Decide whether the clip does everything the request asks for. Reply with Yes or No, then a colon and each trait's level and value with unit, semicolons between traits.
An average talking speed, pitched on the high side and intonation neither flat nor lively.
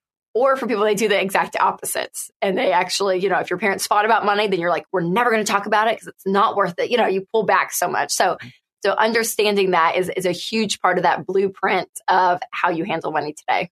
No: fast, 260 wpm; high, 195 Hz; average, 3.0 semitones